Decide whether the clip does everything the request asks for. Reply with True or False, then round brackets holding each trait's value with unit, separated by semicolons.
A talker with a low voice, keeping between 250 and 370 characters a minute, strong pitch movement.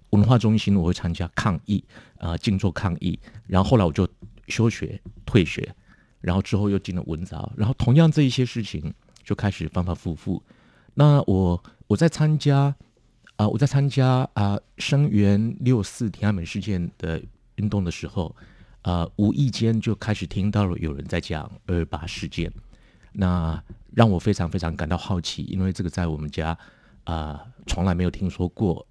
False (100 Hz; 265 characters per minute; 4.3 semitones)